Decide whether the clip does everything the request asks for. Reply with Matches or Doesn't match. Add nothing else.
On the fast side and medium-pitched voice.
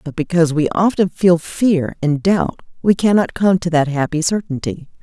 Doesn't match